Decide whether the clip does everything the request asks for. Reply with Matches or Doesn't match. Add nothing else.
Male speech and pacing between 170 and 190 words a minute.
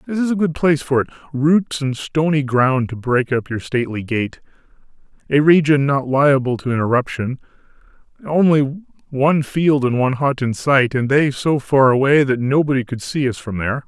Matches